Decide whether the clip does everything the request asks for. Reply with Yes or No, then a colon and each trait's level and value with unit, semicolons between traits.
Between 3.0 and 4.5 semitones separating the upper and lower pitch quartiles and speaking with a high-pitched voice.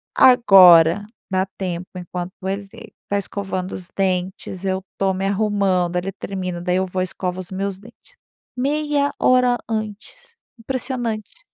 Yes: average, 3.7 semitones; high, 195 Hz